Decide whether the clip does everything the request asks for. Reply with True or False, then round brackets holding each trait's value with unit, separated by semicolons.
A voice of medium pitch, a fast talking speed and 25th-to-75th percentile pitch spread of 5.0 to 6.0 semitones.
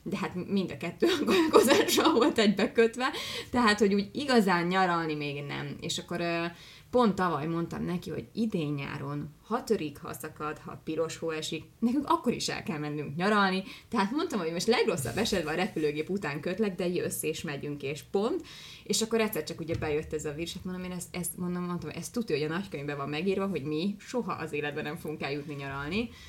True (175 Hz; 200 wpm; 5.3 semitones)